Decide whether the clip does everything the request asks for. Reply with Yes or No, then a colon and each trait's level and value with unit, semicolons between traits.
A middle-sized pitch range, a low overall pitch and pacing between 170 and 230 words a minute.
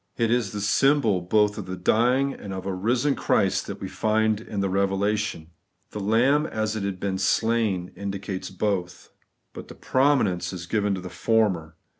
Yes: average, 3.0 semitones; low, 105 Hz; average, 190 wpm